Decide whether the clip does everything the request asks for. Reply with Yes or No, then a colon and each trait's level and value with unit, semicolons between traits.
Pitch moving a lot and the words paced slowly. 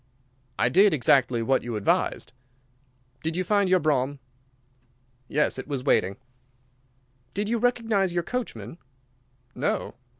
Yes: wide, 7.7 semitones; slow, 125 wpm